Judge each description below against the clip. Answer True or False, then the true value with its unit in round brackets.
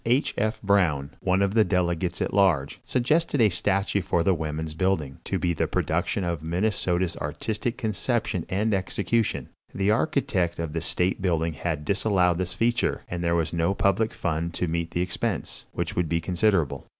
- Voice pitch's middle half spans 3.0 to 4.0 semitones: True (3.3 semitones)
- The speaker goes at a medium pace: True (175 wpm)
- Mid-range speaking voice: False (90 Hz)